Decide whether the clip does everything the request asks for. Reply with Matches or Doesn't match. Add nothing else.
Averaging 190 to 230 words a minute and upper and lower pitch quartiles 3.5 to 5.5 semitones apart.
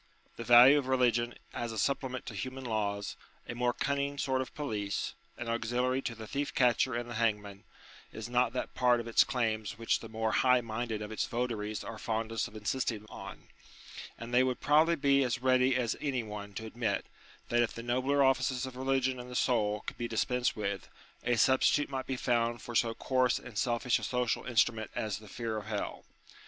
Doesn't match